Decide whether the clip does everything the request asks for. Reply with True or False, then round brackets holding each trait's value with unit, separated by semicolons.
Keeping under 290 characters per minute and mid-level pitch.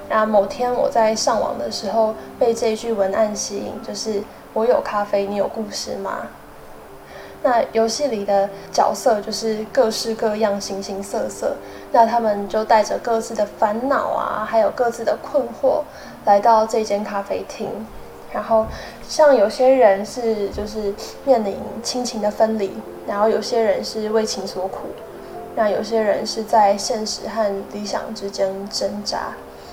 False (230 characters per minute; 220 Hz)